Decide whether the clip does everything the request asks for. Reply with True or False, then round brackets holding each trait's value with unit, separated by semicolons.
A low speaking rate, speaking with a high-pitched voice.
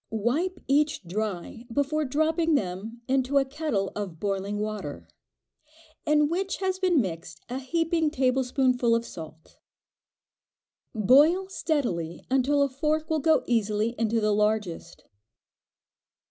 True (120 wpm; 255 Hz)